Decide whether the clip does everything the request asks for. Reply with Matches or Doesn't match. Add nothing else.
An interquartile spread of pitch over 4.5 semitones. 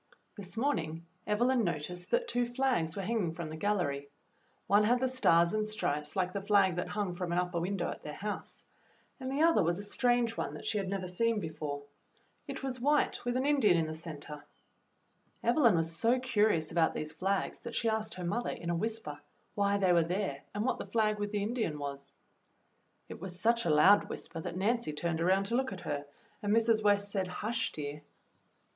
Matches